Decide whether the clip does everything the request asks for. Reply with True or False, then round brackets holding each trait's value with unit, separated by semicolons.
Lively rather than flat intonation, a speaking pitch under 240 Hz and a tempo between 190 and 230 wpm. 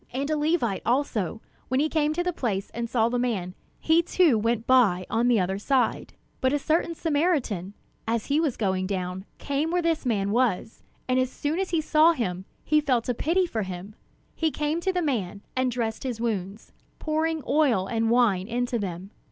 False (6.7 semitones; 245 Hz; 200 wpm)